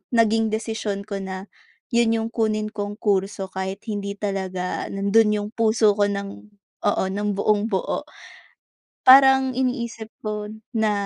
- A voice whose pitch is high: Yes, high, 210 Hz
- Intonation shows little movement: Yes, narrow, 2.0 semitones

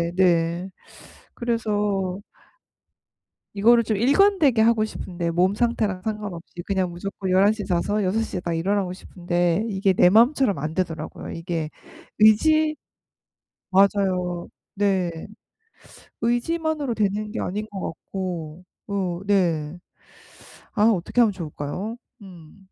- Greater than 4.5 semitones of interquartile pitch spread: No, average, 3.6 semitones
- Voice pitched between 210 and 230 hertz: No, high, 195 Hz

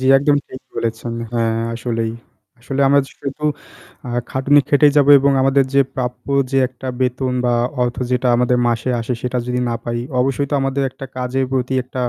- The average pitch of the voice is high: No, low, 130 Hz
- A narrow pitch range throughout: Yes, narrow, 1.7 semitones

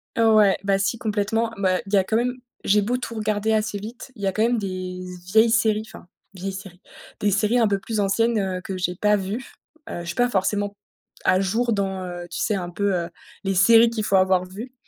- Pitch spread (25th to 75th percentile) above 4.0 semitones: No, average, 2.8 semitones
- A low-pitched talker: No, high, 200 Hz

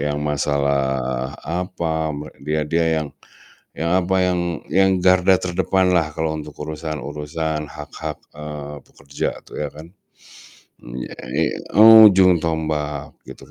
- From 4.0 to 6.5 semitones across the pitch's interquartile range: No, average, 3.3 semitones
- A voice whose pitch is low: Yes, very low, 80 Hz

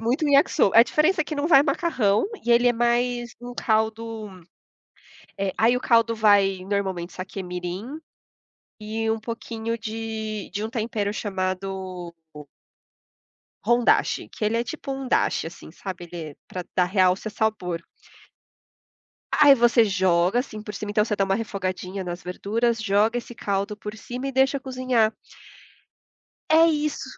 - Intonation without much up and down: No, average, 3.8 semitones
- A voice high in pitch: Yes, high, 220 Hz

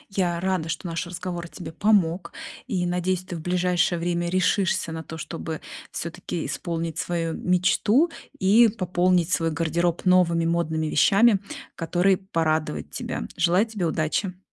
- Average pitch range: No, narrow, 1.9 semitones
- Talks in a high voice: No, medium, 175 Hz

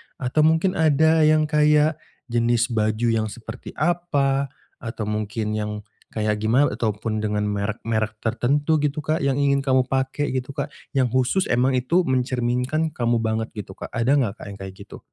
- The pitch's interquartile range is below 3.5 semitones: No, average, 4.7 semitones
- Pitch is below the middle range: Yes, low, 125 Hz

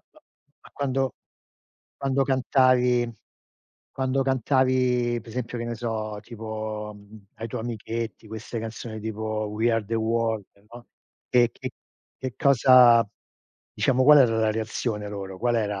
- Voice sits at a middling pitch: No, low, 115 Hz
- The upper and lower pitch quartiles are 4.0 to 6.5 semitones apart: No, narrow, 2.6 semitones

